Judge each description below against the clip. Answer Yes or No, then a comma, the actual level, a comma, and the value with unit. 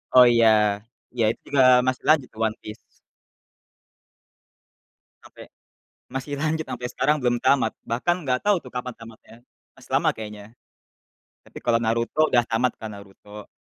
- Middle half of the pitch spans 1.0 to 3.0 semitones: No, average, 3.4 semitones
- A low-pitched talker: Yes, low, 125 Hz